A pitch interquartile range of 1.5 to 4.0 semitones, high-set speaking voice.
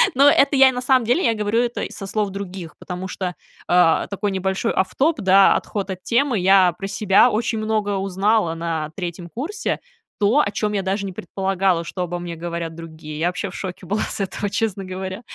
Yes: average, 3.3 semitones; high, 195 Hz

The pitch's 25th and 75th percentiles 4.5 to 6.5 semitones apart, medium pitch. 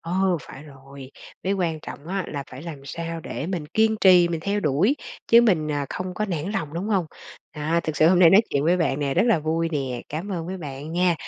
No: average, 4.0 semitones; medium, 165 Hz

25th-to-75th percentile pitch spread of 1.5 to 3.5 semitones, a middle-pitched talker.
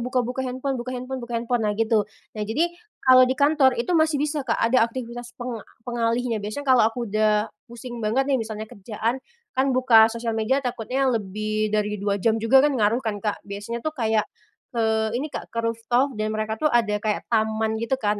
No: average, 2.9 semitones; high, 230 Hz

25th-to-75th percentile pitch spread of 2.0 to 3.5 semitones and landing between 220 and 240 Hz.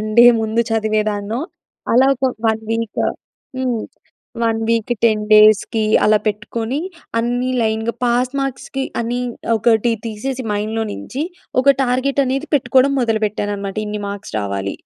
Yes: average, 2.7 semitones; high, 225 Hz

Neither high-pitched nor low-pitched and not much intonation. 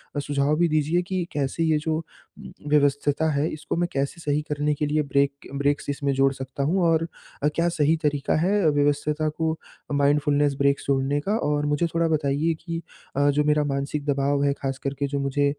Yes: medium, 145 Hz; narrow, 1.9 semitones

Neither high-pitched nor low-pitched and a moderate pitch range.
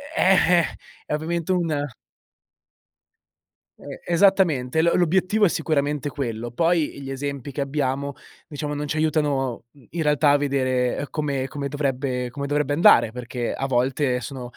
Yes: medium, 145 Hz; average, 3.1 semitones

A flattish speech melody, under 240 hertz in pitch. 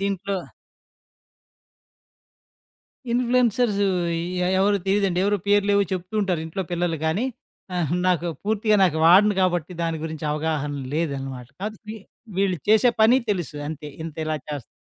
No: average, 4.4 semitones; medium, 185 Hz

